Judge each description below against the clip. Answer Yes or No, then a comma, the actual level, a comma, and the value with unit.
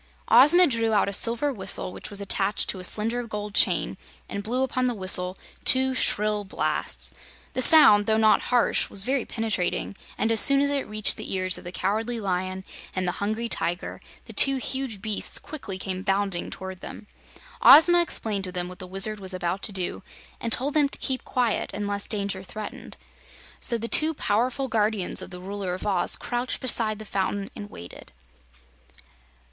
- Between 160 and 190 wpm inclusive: Yes, average, 185 wpm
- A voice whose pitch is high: Yes, high, 210 Hz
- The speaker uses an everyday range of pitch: Yes, average, 4.1 semitones